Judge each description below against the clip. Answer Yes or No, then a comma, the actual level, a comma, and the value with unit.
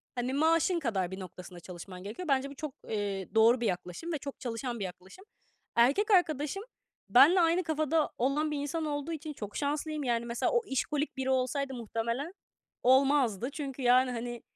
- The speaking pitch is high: Yes, very high, 265 Hz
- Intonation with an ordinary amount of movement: Yes, average, 4.7 semitones